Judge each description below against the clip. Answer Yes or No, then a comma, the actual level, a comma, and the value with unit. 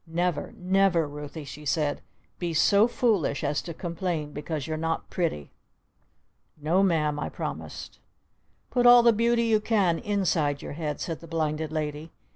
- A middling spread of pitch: Yes, average, 4.5 semitones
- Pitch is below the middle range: No, medium, 165 Hz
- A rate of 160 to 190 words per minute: No, average, 150 wpm